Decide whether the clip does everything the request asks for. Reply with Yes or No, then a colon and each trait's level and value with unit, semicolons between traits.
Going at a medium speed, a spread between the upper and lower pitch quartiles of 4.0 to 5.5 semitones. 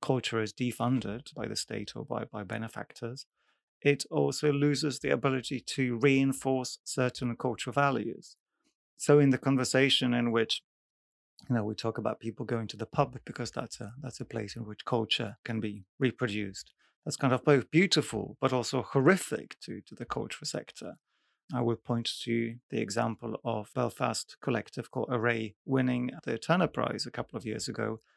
No: average, 175 wpm; average, 3.0 semitones